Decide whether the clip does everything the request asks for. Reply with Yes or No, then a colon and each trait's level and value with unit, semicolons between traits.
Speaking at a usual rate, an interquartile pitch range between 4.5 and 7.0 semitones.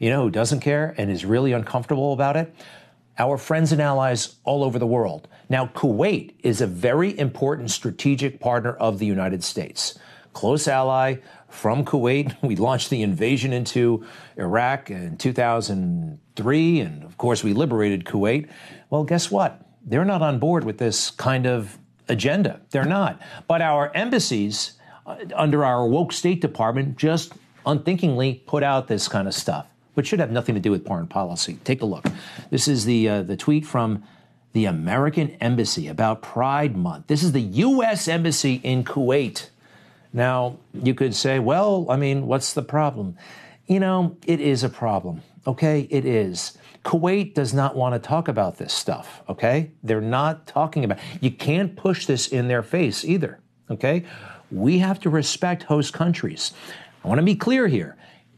Yes: average, 170 wpm; average, 4.9 semitones